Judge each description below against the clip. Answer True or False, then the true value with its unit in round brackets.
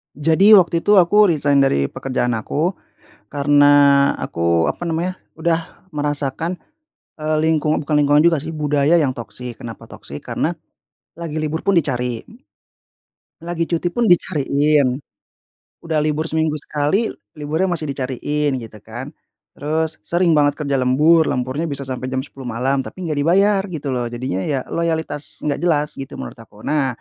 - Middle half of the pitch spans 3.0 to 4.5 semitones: True (3.4 semitones)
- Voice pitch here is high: False (150 Hz)